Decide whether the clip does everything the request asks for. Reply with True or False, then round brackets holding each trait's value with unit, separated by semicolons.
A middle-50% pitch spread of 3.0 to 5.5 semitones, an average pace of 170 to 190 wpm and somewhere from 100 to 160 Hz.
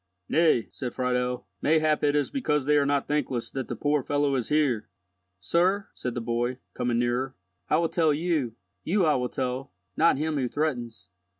True (4.0 semitones; 175 wpm; 135 Hz)